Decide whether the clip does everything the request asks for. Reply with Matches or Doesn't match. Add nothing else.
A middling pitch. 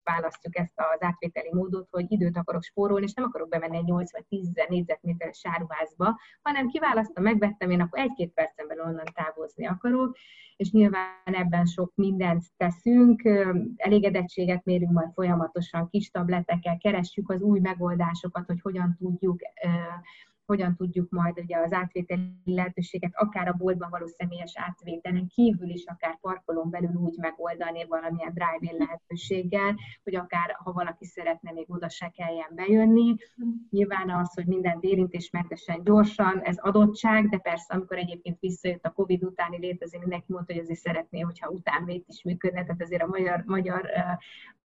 Matches